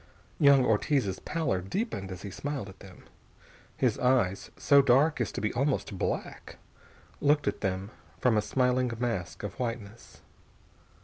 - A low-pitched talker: Yes, low, 120 Hz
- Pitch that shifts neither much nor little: No, wide, 5.8 semitones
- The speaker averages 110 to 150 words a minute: Yes, average, 145 wpm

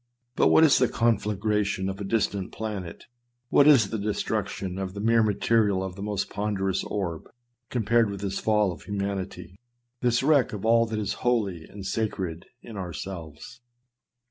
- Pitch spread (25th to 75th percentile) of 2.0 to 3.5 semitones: Yes, average, 2.9 semitones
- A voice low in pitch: Yes, low, 100 Hz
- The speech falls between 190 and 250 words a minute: No, average, 165 wpm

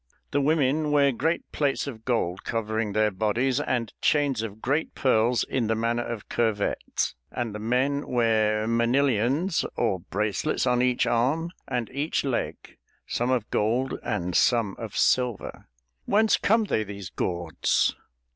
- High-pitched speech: No, low, 120 Hz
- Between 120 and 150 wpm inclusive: Yes, average, 145 wpm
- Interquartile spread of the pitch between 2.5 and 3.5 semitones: No, average, 4.0 semitones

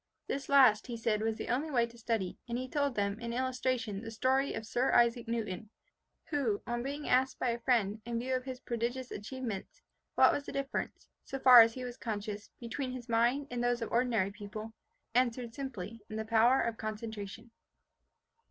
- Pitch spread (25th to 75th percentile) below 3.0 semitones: Yes, narrow, 2.6 semitones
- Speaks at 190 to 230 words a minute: Yes, average, 195 wpm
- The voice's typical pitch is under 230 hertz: No, high, 235 Hz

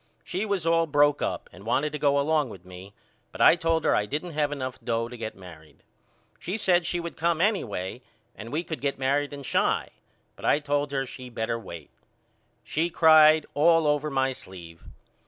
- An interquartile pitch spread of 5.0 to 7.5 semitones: Yes, wide, 5.6 semitones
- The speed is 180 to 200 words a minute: Yes, average, 195 wpm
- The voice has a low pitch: No, medium, 145 Hz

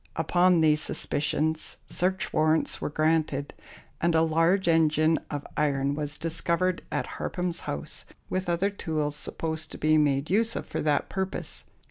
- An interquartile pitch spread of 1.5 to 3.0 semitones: Yes, narrow, 2.4 semitones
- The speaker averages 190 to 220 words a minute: No, average, 150 wpm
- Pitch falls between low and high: Yes, medium, 160 Hz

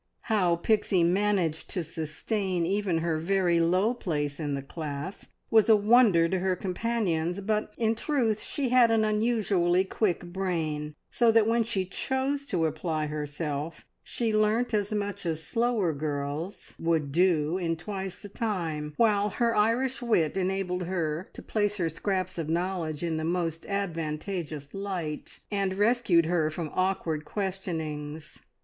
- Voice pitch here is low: No, medium, 185 Hz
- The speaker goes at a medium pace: Yes, average, 150 wpm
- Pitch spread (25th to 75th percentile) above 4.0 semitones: Yes, average, 4.6 semitones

